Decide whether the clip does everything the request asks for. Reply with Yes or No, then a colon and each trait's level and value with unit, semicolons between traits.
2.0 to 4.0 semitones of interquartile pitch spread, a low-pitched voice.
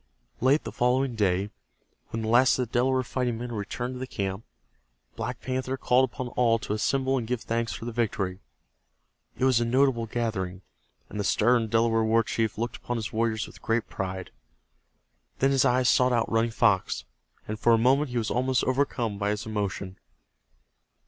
Yes: narrow, 2.6 semitones; low, 115 Hz